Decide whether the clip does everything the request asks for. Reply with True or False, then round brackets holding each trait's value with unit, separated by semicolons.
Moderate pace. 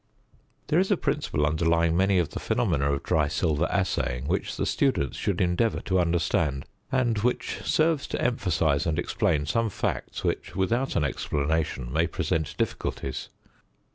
True (155 wpm)